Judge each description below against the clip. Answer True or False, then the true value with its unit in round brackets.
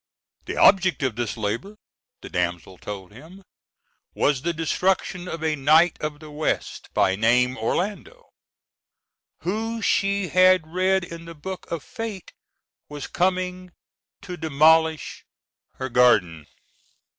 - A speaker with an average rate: False (125 wpm)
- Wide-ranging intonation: True (6.3 semitones)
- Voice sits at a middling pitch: True (160 Hz)